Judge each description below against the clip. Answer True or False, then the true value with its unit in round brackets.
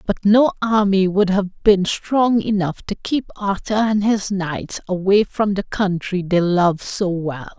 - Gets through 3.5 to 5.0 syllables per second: True (4.0 syllables/s)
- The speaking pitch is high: True (195 Hz)